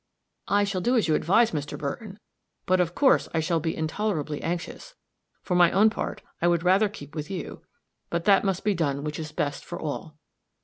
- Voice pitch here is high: No, medium, 175 Hz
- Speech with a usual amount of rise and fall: Yes, average, 4.4 semitones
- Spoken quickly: Yes, fast, 210 wpm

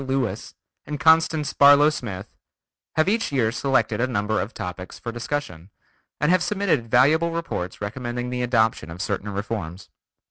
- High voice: No, low, 120 Hz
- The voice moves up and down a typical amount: No, wide, 6.1 semitones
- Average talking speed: Yes, average, 150 wpm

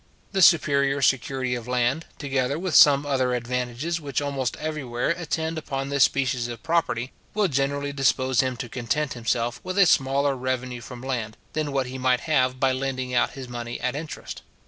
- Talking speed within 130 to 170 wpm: No, average, 180 wpm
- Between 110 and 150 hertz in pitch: Yes, low, 135 Hz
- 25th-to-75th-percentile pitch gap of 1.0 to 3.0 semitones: Yes, narrow, 2.4 semitones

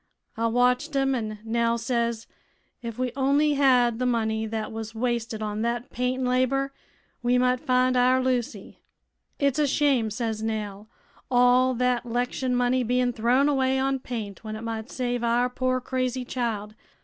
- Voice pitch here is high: Yes, high, 245 Hz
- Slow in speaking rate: No, average, 165 wpm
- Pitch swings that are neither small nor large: No, narrow, 2.0 semitones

